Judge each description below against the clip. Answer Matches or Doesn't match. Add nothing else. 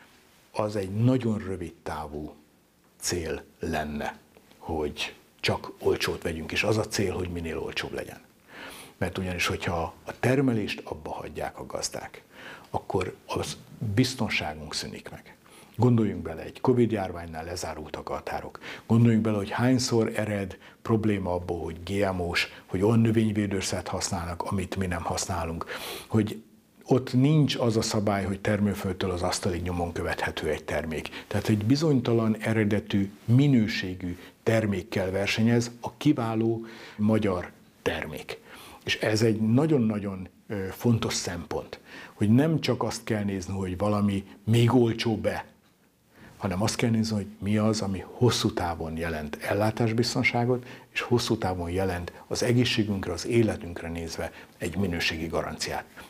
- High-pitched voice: Doesn't match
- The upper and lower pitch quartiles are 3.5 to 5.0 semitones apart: Matches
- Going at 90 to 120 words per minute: Doesn't match